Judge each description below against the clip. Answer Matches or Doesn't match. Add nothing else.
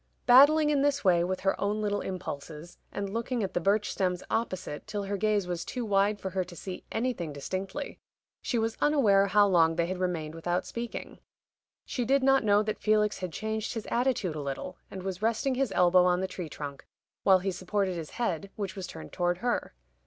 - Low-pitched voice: Doesn't match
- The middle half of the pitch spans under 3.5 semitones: Doesn't match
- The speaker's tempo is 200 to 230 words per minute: Matches